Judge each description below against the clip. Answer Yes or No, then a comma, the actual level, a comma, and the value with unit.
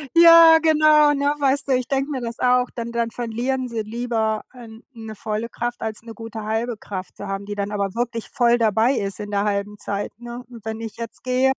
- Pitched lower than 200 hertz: No, high, 230 Hz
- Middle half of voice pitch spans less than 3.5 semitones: Yes, average, 2.7 semitones